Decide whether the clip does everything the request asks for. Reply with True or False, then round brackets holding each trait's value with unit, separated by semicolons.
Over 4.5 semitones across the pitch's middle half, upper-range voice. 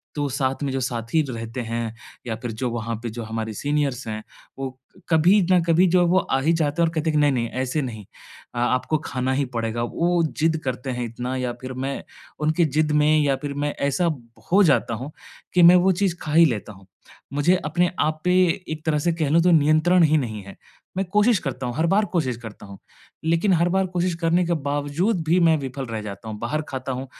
False (5.3 semitones; 145 Hz)